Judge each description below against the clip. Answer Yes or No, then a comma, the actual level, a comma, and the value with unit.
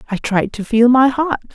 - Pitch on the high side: Yes, high, 240 Hz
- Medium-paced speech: No, fast, 235 wpm